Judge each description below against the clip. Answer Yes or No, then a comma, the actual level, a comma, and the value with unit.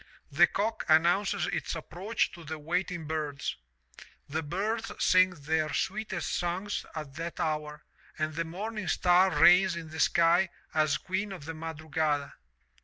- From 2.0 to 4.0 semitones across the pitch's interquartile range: Yes, average, 3.4 semitones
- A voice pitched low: No, medium, 165 Hz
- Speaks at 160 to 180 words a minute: No, average, 145 wpm